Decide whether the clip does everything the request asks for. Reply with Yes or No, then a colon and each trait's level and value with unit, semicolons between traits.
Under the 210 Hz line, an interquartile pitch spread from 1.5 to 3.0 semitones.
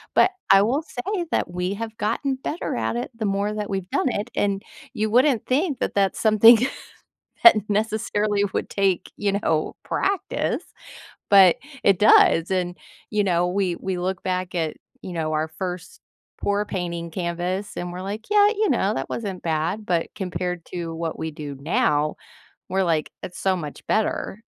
No: high, 190 Hz; average, 3.6 semitones